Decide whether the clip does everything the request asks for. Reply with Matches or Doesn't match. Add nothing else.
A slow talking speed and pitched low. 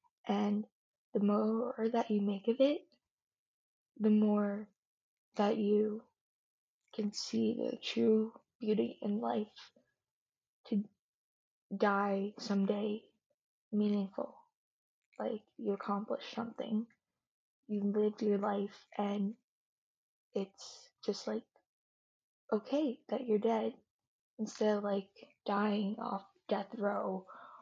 Doesn't match